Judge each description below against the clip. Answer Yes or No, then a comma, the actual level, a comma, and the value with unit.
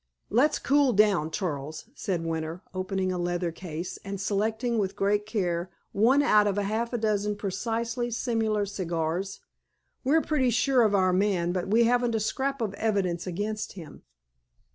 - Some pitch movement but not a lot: Yes, average, 3.8 semitones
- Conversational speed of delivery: Yes, average, 160 wpm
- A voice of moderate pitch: No, high, 205 Hz